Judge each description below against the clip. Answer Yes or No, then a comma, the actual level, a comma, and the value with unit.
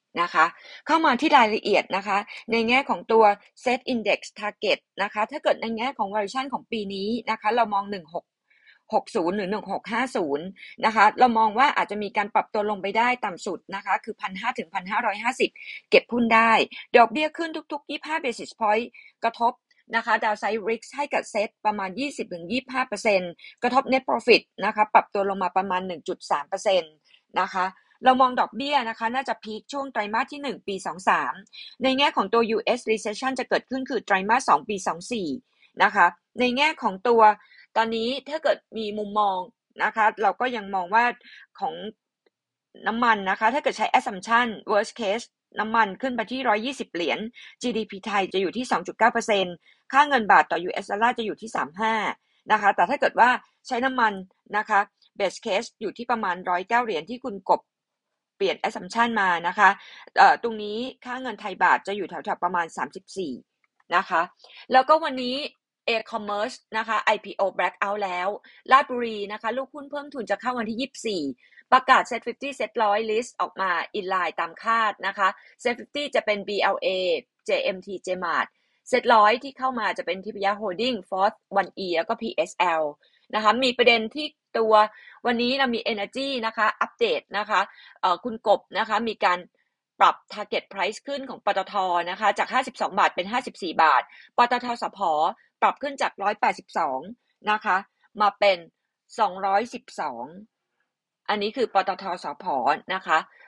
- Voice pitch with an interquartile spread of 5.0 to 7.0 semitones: No, average, 3.8 semitones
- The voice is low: No, high, 220 Hz